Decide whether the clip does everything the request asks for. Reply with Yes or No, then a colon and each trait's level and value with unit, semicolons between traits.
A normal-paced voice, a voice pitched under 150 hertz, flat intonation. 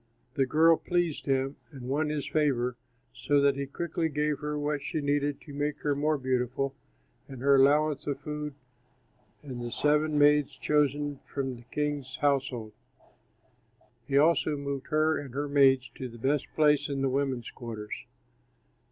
Yes: average, 160 wpm; medium, 140 Hz; narrow, 1.9 semitones